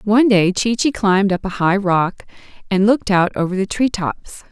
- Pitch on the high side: Yes, high, 200 Hz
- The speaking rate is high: Yes, fast, 215 wpm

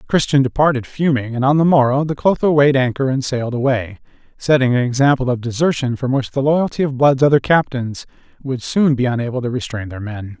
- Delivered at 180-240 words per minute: Yes, average, 200 wpm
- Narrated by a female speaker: No, male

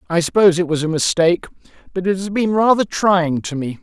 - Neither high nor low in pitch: Yes, medium, 175 Hz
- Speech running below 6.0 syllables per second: No, 6.1 syllables/s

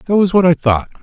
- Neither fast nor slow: No, fast, 295 wpm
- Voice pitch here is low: No, medium, 160 Hz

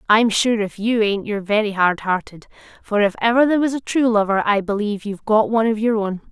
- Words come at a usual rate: No, fast, 235 wpm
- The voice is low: No, high, 215 Hz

